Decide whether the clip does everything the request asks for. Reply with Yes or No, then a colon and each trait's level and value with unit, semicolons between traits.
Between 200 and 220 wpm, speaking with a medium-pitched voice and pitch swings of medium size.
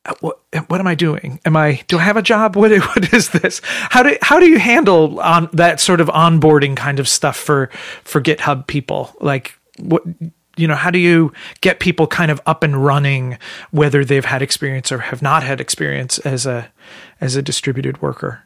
Yes: fast, 205 wpm; medium, 155 Hz; average, 3.9 semitones